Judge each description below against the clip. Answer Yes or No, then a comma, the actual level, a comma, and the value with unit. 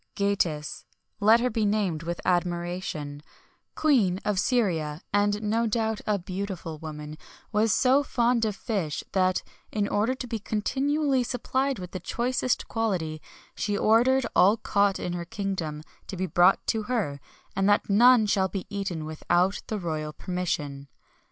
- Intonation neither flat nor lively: Yes, average, 4.5 semitones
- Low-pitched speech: No, high, 200 Hz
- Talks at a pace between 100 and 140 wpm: No, average, 150 wpm